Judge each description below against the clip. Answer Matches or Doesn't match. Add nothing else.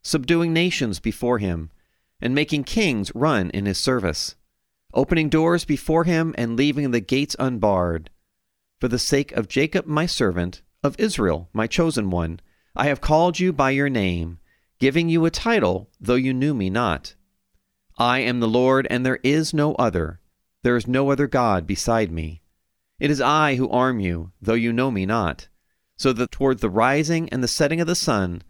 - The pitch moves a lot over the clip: Matches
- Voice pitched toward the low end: Matches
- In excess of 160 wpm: Matches